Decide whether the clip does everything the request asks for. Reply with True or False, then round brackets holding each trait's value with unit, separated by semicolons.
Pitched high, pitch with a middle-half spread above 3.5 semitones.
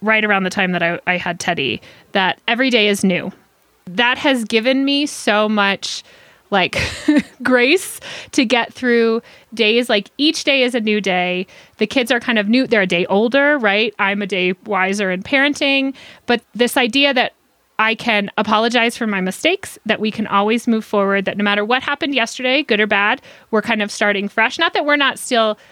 True (225 Hz; 3.9 semitones)